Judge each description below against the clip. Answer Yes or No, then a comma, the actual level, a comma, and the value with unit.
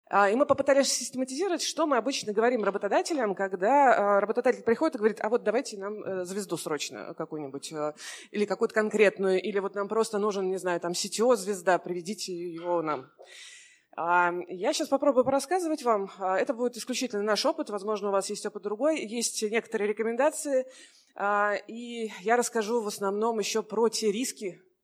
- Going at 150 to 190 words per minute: Yes, average, 155 wpm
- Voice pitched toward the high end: Yes, high, 215 Hz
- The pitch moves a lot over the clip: No, average, 4.3 semitones